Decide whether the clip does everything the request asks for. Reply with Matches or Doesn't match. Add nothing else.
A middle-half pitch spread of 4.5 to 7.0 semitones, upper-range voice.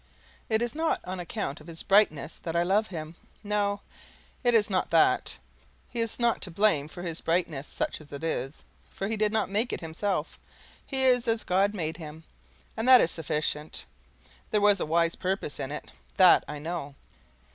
Doesn't match